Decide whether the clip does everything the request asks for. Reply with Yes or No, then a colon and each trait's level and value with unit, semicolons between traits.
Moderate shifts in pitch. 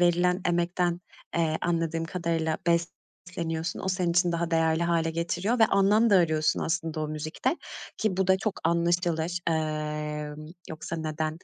No: narrow, 1.9 semitones